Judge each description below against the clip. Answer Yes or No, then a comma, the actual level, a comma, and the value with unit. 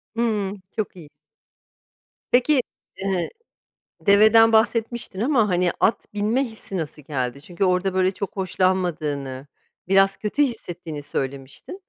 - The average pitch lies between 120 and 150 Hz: No, high, 195 Hz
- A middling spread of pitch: Yes, average, 4.7 semitones